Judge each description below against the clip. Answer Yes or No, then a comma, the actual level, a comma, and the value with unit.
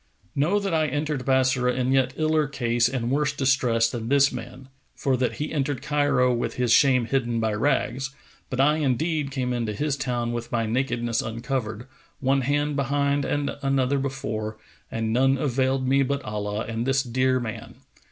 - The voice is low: Yes, low, 130 Hz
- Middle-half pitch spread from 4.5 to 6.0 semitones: No, average, 2.8 semitones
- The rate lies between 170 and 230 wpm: Yes, average, 175 wpm